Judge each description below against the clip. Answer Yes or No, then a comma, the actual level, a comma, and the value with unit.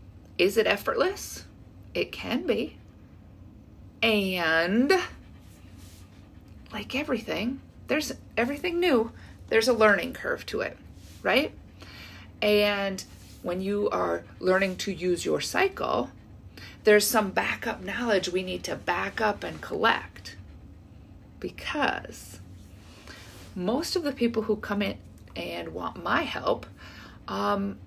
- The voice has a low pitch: No, medium, 160 Hz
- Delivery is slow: Yes, slow, 110 wpm